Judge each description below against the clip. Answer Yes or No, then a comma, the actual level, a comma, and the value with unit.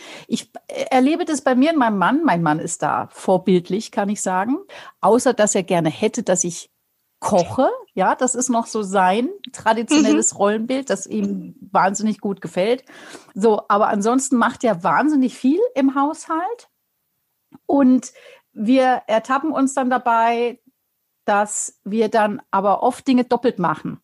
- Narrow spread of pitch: No, average, 4.8 semitones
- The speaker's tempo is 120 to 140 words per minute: No, average, 150 wpm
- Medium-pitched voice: No, high, 235 Hz